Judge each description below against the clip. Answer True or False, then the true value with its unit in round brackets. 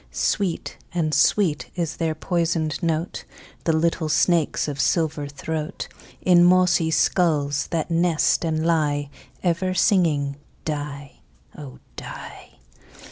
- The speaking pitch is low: False (160 Hz)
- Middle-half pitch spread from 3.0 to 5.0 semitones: False (2.6 semitones)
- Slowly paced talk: True (115 wpm)